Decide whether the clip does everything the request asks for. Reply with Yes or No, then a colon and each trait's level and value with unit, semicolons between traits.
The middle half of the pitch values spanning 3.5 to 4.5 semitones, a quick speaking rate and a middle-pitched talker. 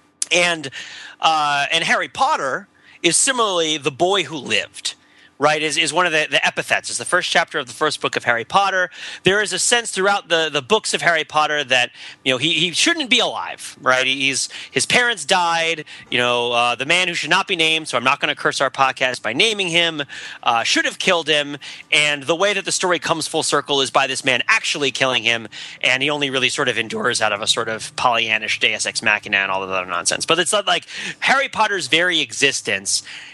No: average, 5.2 semitones; fast, 225 wpm; medium, 155 Hz